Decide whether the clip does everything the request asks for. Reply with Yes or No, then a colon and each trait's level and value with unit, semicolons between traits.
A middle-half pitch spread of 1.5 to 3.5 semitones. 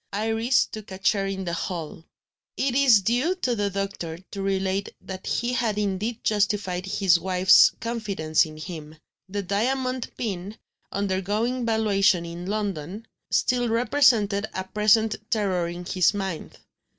Yes: average, 3.2 semitones